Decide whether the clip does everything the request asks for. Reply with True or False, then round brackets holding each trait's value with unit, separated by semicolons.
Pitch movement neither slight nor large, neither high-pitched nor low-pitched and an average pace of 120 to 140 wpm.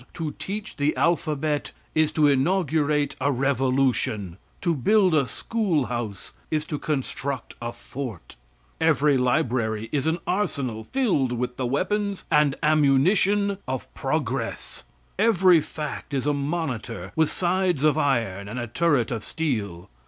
True (4.8 semitones; 145 Hz; 135 wpm)